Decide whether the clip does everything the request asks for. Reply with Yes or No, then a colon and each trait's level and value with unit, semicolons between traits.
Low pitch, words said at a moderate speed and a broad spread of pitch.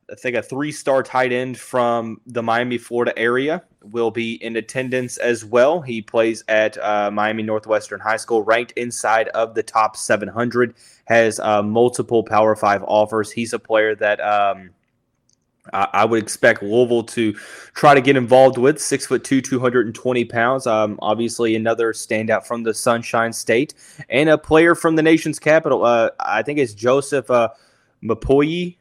No: low, 115 Hz; average, 170 wpm; average, 2.8 semitones